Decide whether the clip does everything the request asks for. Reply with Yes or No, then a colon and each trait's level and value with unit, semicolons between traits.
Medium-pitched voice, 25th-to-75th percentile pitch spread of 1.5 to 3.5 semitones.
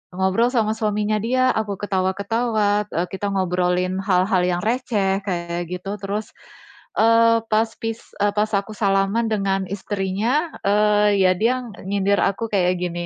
No: high, 205 Hz; narrow, 2.5 semitones